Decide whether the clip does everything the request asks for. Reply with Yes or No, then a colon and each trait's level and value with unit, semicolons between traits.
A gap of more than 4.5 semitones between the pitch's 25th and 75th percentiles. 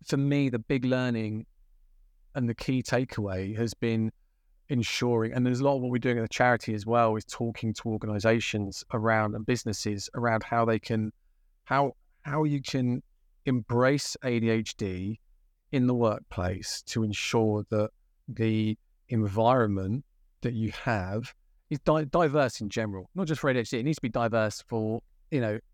No: average, 2.9 semitones